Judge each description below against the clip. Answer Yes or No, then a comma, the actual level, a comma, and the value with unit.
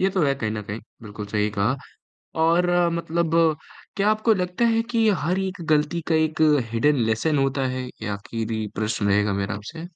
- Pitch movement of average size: No, wide, 8.0 semitones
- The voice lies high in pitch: No, medium, 140 Hz